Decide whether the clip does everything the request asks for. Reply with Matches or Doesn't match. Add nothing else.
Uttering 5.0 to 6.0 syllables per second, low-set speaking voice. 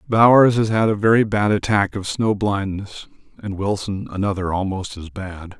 Doesn't match